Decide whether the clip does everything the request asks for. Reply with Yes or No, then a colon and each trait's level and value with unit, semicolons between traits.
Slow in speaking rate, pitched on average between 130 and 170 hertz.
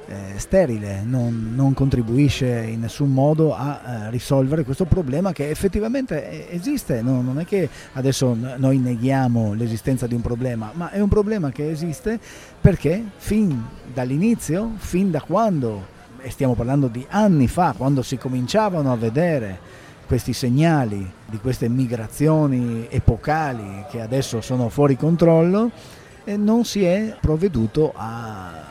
No: average, 140 wpm; low, 135 Hz